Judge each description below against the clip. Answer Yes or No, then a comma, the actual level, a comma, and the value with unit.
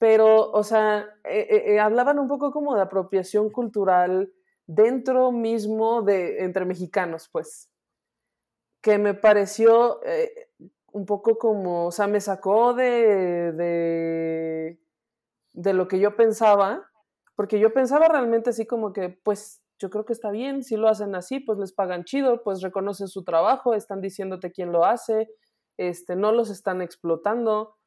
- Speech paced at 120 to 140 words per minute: No, average, 155 wpm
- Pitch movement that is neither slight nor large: Yes, average, 3.3 semitones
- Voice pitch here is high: Yes, high, 210 Hz